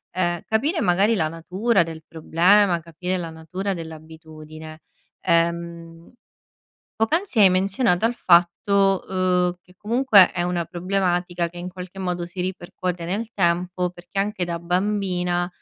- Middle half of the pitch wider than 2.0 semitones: Yes, narrow, 2.4 semitones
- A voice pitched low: No, medium, 180 Hz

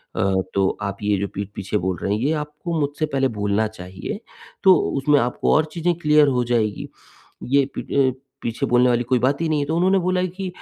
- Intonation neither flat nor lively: No, wide, 6.7 semitones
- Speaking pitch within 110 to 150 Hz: Yes, low, 135 Hz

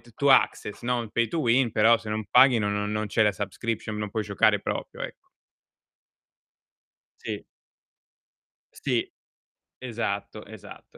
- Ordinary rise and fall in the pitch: No, narrow, 2.1 semitones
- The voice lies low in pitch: Yes, low, 110 Hz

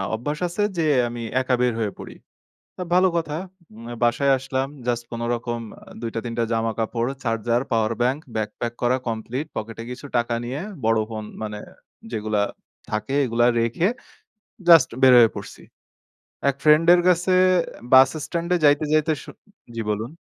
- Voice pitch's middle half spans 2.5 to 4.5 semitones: Yes, average, 4.1 semitones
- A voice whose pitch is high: No, low, 120 Hz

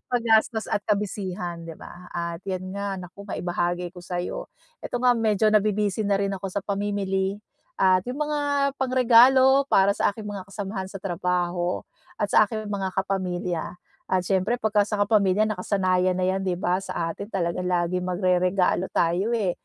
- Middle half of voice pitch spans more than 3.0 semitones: No, average, 2.7 semitones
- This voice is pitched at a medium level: No, high, 195 Hz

